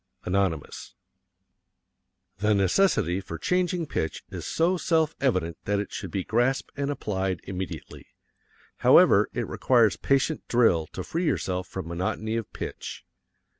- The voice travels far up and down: Yes, wide, 7.2 semitones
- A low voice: Yes, low, 105 Hz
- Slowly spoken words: Yes, slow, 130 wpm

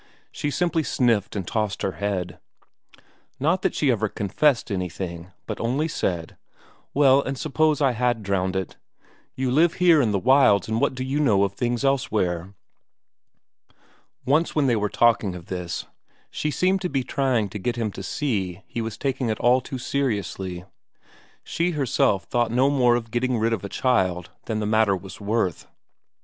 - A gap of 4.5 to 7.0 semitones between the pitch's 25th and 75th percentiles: Yes, wide, 5.5 semitones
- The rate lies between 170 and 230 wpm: Yes, average, 175 wpm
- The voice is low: Yes, low, 115 Hz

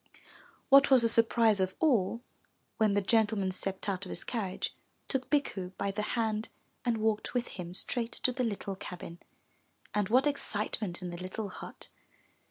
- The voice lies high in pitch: Yes, high, 215 Hz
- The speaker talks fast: No, average, 170 wpm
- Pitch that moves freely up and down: No, average, 3.8 semitones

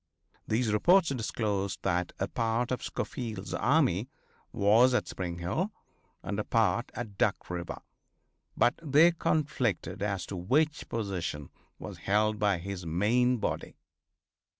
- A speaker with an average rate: No, slow, 130 wpm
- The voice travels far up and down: No, average, 4.5 semitones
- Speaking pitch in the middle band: No, low, 110 Hz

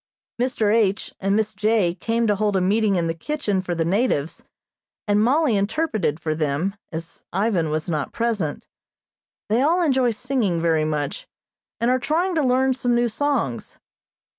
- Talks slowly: No, average, 165 wpm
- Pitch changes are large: Yes, wide, 6.6 semitones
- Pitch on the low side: No, high, 210 Hz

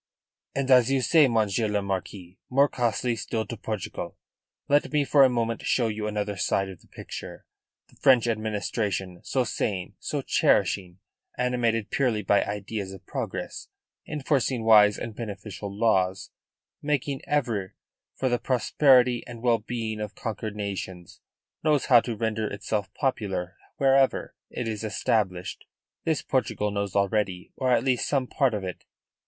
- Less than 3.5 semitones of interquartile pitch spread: No, average, 3.8 semitones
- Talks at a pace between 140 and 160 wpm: Yes, average, 150 wpm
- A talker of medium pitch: No, low, 110 Hz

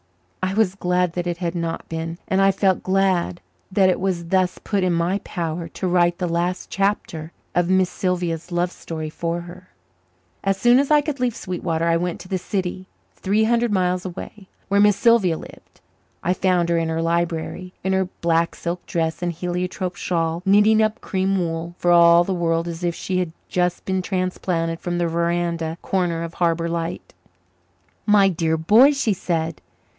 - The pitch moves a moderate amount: No, narrow, 2.1 semitones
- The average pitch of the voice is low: No, medium, 180 Hz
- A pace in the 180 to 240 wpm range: Yes, average, 185 wpm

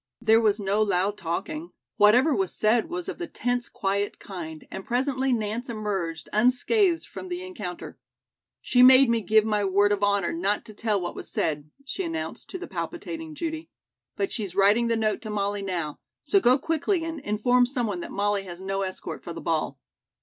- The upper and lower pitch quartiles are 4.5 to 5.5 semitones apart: Yes, average, 5.1 semitones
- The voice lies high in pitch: Yes, high, 215 Hz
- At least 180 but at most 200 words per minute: Yes, average, 190 wpm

